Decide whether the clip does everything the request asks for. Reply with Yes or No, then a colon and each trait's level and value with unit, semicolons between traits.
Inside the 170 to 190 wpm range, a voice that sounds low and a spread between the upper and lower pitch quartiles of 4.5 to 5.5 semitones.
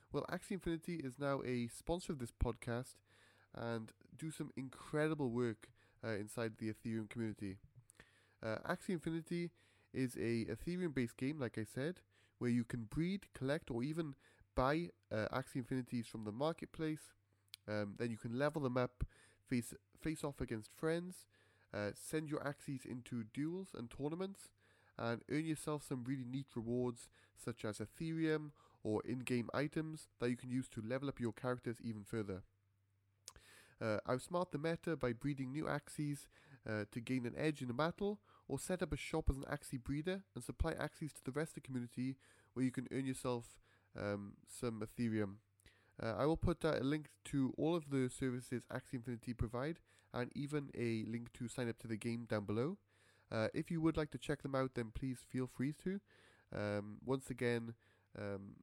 Yes: average, 180 wpm; low, 125 Hz; average, 5.0 semitones